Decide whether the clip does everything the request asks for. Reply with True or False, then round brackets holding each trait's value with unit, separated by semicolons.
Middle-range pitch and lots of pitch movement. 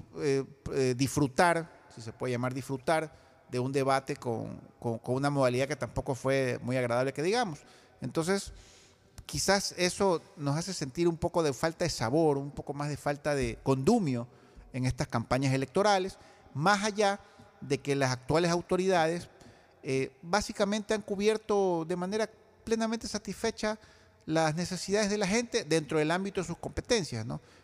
True (155 Hz; 6.5 semitones)